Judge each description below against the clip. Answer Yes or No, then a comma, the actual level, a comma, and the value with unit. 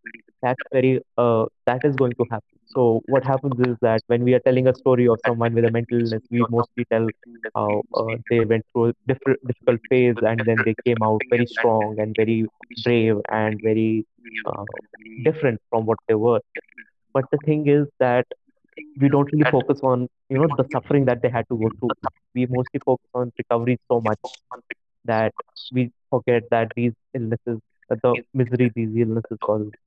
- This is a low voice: Yes, low, 120 Hz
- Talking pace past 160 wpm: Yes, average, 190 wpm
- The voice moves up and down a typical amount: No, narrow, 2.3 semitones